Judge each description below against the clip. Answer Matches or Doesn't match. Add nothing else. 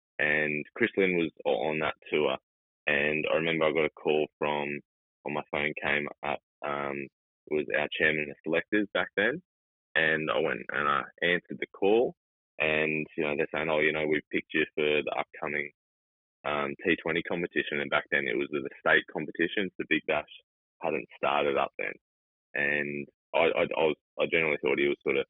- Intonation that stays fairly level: Matches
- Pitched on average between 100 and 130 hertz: Doesn't match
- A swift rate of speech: Doesn't match